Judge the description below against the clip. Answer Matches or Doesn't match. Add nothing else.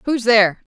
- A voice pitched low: Doesn't match